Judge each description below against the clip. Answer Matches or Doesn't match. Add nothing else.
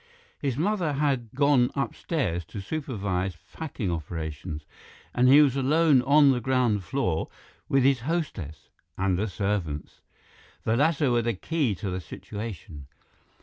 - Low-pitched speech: Matches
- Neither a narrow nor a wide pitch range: Doesn't match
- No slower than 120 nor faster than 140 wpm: Matches